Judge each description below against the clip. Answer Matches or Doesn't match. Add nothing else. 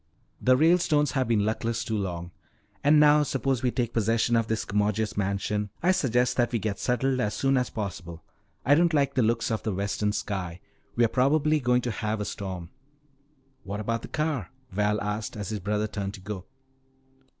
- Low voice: Matches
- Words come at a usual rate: Matches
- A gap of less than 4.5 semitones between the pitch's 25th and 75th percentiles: Matches